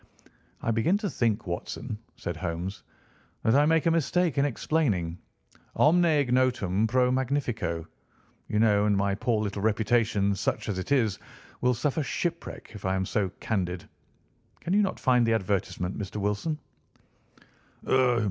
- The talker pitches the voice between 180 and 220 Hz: No, low, 110 Hz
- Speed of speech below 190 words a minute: Yes, average, 150 wpm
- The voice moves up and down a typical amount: No, wide, 5.9 semitones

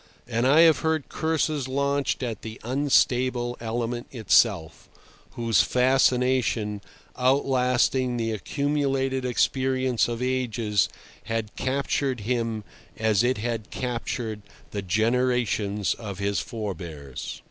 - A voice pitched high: No, low, 120 Hz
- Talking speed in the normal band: No, slow, 105 wpm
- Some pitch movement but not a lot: Yes, average, 3.0 semitones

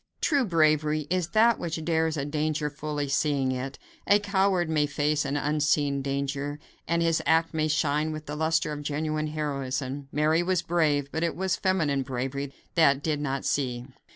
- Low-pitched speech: No, medium, 150 Hz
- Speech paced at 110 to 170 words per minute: No, average, 180 wpm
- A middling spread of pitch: No, narrow, 2.3 semitones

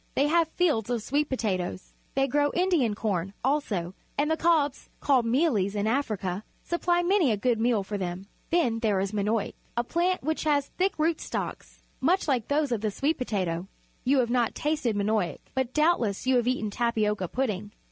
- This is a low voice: No, high, 245 Hz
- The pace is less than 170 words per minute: No, average, 185 wpm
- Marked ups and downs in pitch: Yes, wide, 6.3 semitones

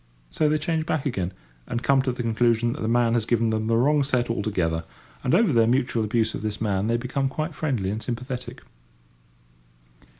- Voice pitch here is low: Yes, low, 120 Hz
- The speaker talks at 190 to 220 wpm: Yes, average, 200 wpm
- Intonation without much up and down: No, average, 3.4 semitones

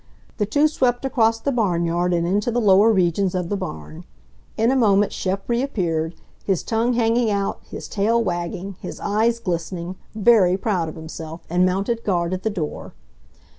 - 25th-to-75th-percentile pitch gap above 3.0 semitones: Yes, average, 4.5 semitones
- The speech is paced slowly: No, average, 170 wpm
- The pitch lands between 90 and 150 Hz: No, high, 195 Hz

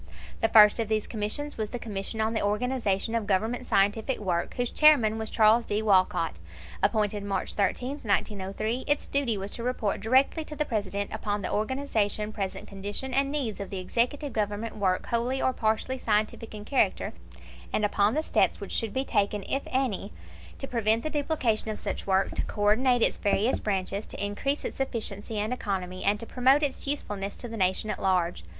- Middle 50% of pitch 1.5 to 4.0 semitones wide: Yes, average, 3.6 semitones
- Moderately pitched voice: No, high, 215 Hz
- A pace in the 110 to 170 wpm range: No, average, 190 wpm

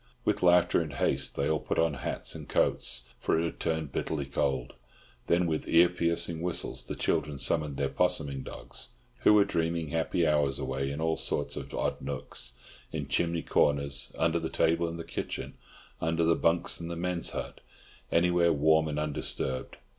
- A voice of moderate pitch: No, very low, 80 Hz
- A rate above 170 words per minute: Yes, average, 180 wpm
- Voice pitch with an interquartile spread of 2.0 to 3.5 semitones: Yes, average, 2.8 semitones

